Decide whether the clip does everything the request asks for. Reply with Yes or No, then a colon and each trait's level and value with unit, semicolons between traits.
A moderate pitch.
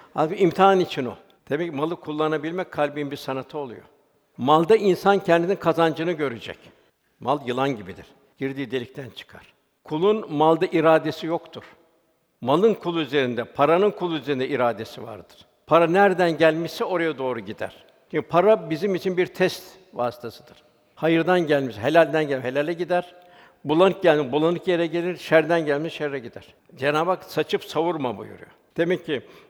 Yes: medium, 160 Hz